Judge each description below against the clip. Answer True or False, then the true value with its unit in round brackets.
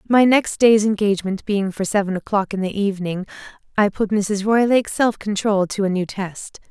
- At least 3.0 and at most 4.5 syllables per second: False (5.2 syllables/s)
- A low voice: False (205 Hz)